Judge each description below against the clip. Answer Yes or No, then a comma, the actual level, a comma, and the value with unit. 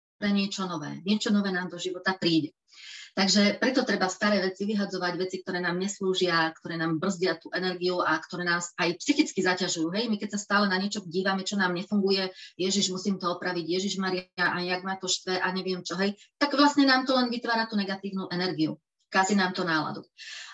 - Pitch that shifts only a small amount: Yes, narrow, 2.1 semitones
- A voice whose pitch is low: No, medium, 185 Hz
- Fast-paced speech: Yes, fast, 200 wpm